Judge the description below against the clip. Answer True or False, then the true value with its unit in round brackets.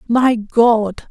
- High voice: True (230 Hz)